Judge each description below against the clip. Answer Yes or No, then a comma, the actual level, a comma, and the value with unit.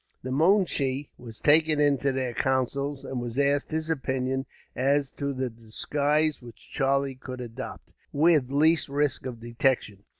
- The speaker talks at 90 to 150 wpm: Yes, average, 145 wpm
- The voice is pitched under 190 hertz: Yes, low, 135 Hz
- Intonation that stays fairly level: Yes, narrow, 2.3 semitones